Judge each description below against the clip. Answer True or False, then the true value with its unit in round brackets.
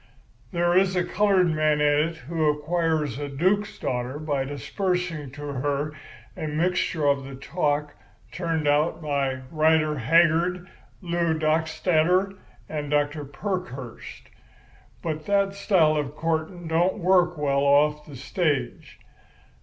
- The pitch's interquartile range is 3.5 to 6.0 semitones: False (3.1 semitones)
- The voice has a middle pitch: True (155 Hz)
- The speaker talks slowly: True (130 wpm)